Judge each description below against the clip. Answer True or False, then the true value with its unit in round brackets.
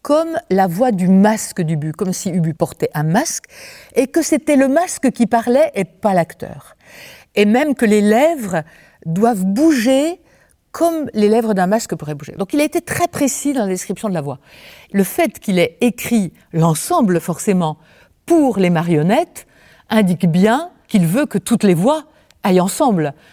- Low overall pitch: False (215 Hz)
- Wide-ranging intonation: True (7.4 semitones)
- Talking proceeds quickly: False (175 wpm)